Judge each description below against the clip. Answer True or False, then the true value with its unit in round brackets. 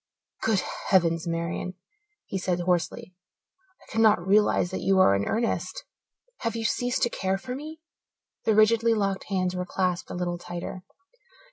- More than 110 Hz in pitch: True (190 Hz)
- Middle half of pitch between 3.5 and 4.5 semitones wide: True (3.9 semitones)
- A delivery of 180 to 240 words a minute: False (155 wpm)